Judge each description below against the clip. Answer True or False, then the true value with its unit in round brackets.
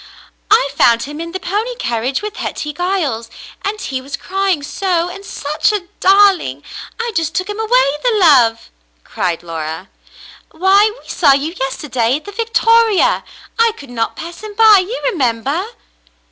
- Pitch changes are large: True (7.7 semitones)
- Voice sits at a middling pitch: False (335 Hz)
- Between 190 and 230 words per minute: False (175 wpm)